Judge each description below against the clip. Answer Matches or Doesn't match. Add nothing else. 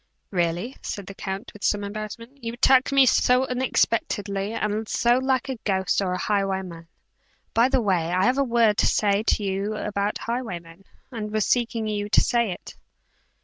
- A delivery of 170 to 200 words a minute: Matches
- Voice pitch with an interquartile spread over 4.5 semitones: Doesn't match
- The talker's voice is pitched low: Doesn't match